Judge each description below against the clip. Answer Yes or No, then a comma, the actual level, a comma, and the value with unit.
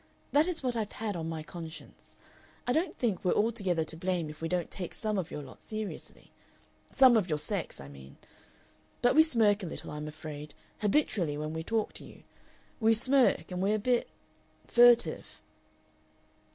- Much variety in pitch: Yes, wide, 6.4 semitones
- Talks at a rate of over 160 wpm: Yes, average, 180 wpm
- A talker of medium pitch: No, high, 195 Hz